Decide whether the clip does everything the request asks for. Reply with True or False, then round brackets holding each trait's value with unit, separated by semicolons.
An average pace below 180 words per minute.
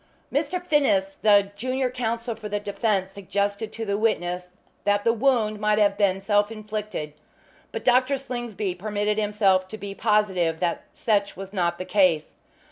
True (160 wpm)